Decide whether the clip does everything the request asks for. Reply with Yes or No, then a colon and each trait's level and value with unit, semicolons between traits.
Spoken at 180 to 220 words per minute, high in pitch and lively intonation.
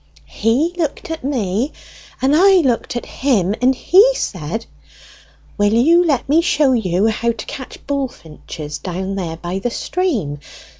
No: average, 150 wpm; high, 240 Hz; wide, 7.4 semitones